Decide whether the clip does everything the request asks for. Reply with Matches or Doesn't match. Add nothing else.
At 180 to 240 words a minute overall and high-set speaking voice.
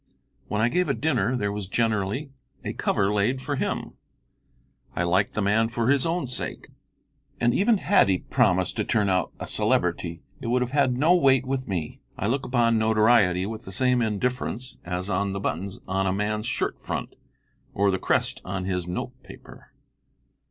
Doesn't match